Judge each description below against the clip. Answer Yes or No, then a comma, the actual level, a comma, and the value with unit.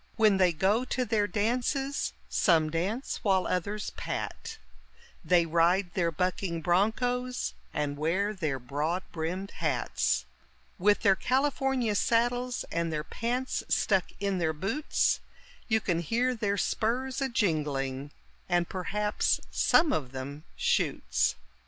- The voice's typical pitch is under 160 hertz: No, high, 195 Hz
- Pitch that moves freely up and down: Yes, wide, 5.9 semitones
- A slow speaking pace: Yes, slow, 125 wpm